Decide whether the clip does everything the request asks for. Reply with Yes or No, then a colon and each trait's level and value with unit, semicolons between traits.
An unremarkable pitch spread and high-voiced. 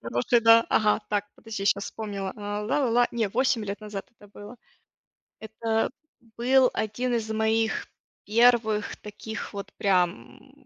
No: narrow, 1.9 semitones; high, 220 Hz